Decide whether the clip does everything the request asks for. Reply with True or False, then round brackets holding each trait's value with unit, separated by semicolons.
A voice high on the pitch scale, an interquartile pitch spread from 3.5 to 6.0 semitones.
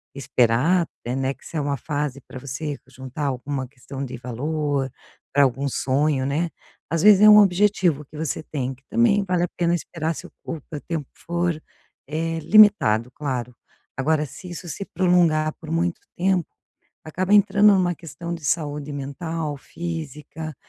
False (155 Hz; 4.1 semitones)